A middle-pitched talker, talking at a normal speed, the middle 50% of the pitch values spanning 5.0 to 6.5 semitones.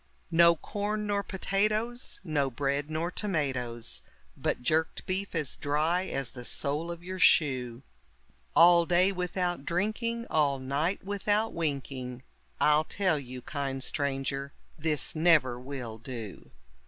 No: medium, 155 Hz; slow, 130 wpm; average, 5.3 semitones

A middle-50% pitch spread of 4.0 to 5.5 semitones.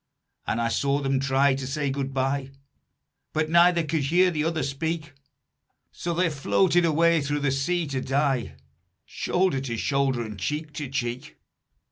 No: average, 3.3 semitones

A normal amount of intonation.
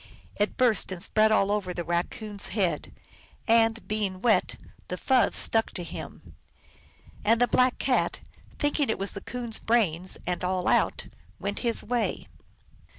Yes: average, 3.8 semitones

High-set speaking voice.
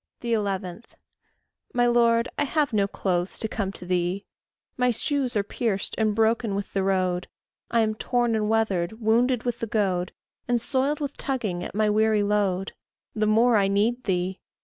Yes: high, 215 Hz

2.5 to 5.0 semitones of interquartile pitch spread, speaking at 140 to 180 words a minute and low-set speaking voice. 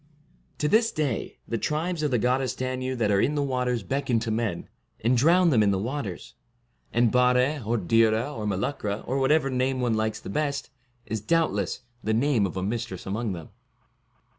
No: average, 4.2 semitones; average, 190 wpm; low, 125 Hz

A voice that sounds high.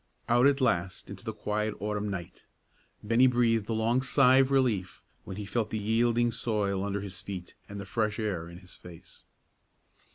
No: low, 105 Hz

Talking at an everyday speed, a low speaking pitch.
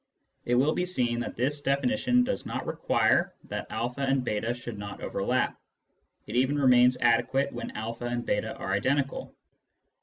Yes: average, 170 wpm; low, 125 Hz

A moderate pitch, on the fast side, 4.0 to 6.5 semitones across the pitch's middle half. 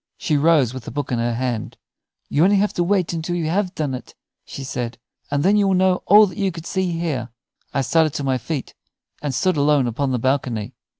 Yes: medium, 150 Hz; fast, 230 wpm; wide, 5.6 semitones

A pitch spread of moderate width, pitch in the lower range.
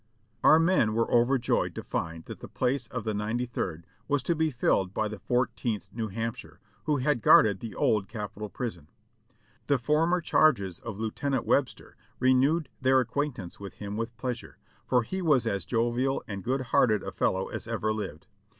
Yes: average, 4.2 semitones; low, 120 Hz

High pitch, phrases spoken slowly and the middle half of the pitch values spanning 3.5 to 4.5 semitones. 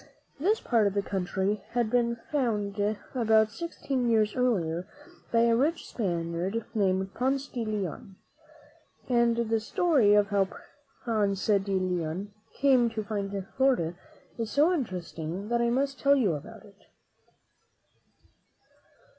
Yes: high, 220 Hz; slow, 130 wpm; average, 4.0 semitones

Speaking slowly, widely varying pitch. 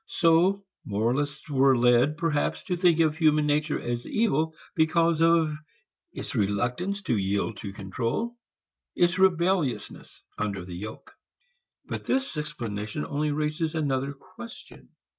Yes: slow, 125 wpm; wide, 5.8 semitones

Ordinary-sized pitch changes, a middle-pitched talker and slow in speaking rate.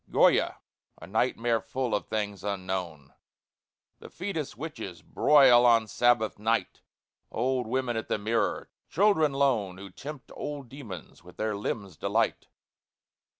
No: average, 4.7 semitones; low, 115 Hz; slow, 130 wpm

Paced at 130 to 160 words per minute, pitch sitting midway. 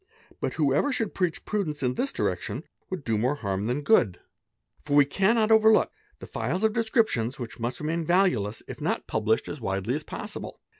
No: average, 195 wpm; medium, 150 Hz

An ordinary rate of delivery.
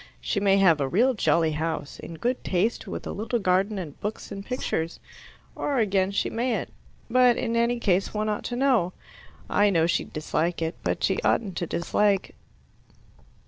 Yes: average, 180 wpm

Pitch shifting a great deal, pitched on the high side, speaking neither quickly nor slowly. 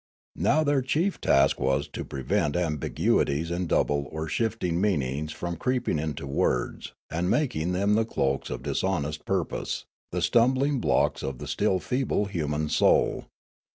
No: wide, 7.2 semitones; very low, 85 Hz; average, 150 wpm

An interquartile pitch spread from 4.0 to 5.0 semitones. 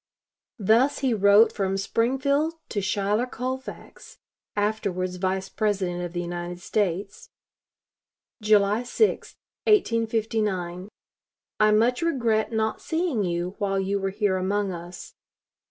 No: average, 3.4 semitones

